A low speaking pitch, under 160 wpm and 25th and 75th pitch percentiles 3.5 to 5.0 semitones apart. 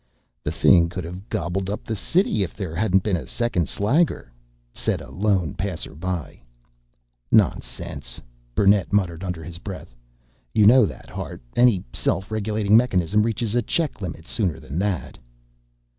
Yes: very low, 95 Hz; average, 150 wpm; average, 4.0 semitones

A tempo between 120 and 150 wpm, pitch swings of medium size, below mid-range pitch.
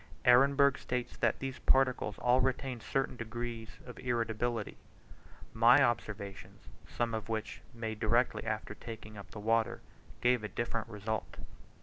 No: average, 145 wpm; narrow, 2.1 semitones; low, 115 Hz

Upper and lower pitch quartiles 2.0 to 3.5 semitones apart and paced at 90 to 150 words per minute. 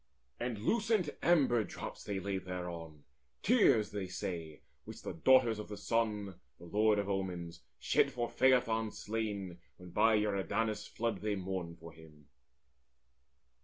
No: average, 4.0 semitones; average, 140 wpm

